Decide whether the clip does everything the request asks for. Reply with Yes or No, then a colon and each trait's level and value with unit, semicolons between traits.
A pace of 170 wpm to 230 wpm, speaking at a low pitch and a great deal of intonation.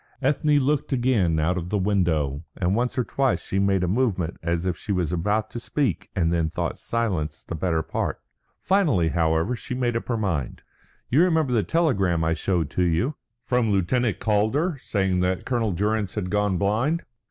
Yes: average, 185 wpm; low, 100 Hz; wide, 6.1 semitones